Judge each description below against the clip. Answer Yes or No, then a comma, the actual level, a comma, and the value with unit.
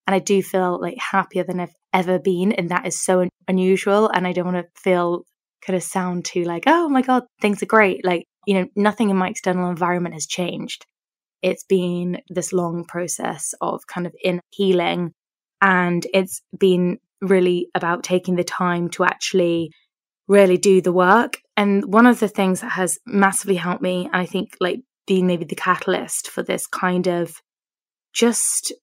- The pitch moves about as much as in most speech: No, narrow, 1.7 semitones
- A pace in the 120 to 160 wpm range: No, average, 185 wpm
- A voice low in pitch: No, medium, 185 Hz